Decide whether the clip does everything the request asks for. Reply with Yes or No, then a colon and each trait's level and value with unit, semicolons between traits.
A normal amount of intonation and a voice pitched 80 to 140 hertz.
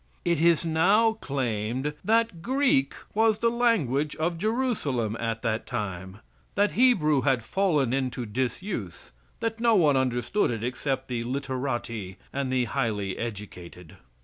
No: wide, 8.8 semitones; low, 135 Hz